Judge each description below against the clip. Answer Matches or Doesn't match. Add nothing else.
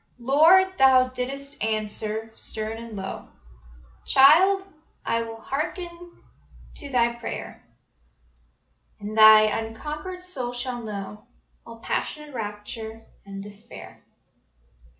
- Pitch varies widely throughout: Doesn't match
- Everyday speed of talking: Doesn't match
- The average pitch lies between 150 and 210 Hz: Doesn't match